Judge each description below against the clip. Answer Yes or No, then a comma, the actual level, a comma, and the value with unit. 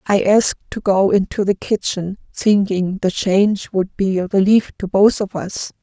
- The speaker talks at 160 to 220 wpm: Yes, average, 185 wpm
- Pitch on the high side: Yes, high, 195 Hz